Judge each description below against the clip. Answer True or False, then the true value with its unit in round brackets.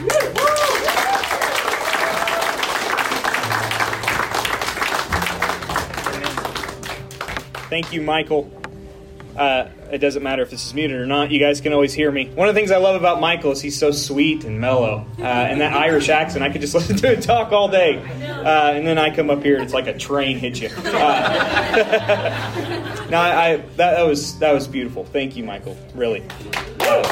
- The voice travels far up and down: False (3.5 semitones)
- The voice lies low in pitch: False (145 Hz)